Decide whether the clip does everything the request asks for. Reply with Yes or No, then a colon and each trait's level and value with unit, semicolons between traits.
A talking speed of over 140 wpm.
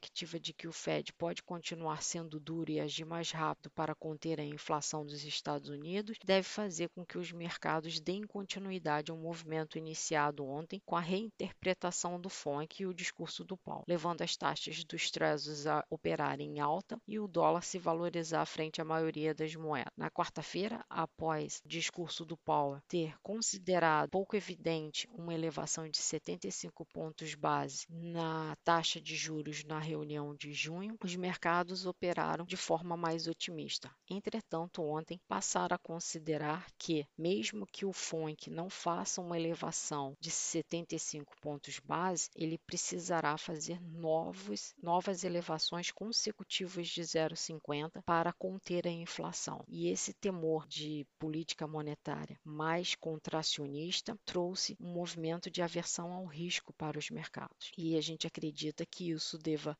Yes: average, 150 wpm